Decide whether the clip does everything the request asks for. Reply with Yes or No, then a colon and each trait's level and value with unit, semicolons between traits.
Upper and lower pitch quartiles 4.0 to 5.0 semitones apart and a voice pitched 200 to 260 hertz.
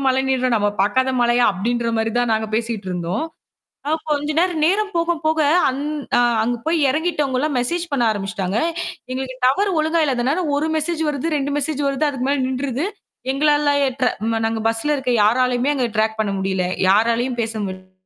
Yes: average, 4.6 semitones; very high, 255 Hz